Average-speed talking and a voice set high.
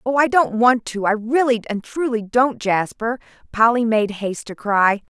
Yes: average, 185 wpm; high, 230 Hz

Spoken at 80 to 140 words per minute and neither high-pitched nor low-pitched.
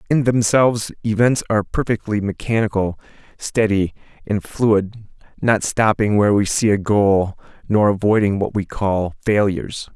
No: slow, 135 wpm; low, 105 Hz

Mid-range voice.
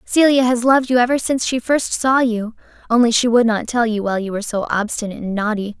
No: high, 235 Hz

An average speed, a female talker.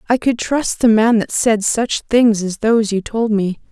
No: fast, 225 wpm; female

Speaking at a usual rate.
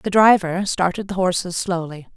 Yes: average, 165 wpm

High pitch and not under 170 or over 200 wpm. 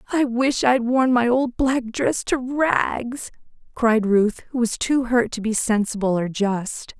Yes: high, 235 Hz; average, 180 wpm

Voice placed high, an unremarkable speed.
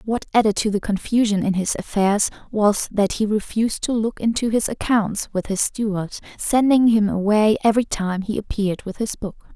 Yes: high, 210 Hz; average, 190 wpm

